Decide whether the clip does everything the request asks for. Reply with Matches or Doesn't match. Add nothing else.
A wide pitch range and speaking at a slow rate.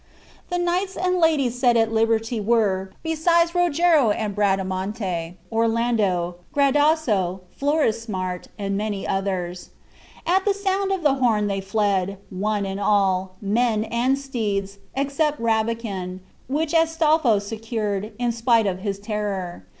Matches